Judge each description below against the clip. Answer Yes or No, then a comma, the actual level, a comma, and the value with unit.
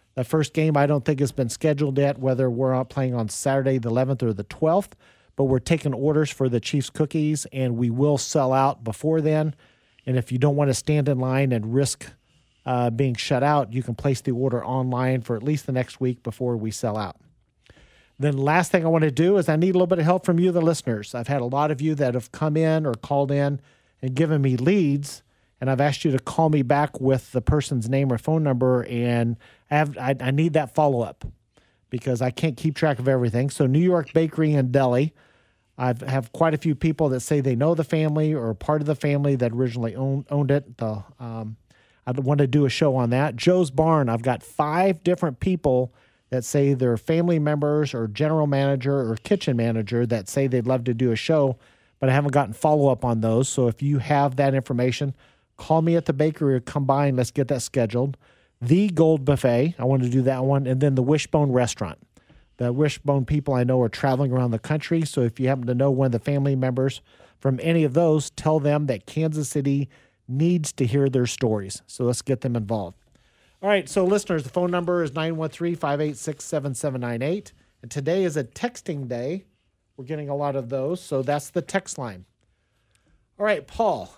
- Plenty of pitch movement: No, average, 3.5 semitones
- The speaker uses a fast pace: Yes, fast, 220 wpm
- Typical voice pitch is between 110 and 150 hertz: Yes, medium, 140 Hz